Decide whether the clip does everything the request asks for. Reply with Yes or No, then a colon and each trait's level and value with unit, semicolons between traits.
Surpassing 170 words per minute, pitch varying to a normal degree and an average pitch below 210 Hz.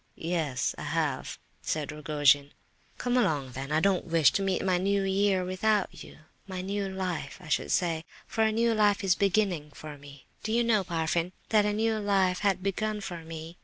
Yes: average, 190 wpm; average, 4.3 semitones; medium, 185 Hz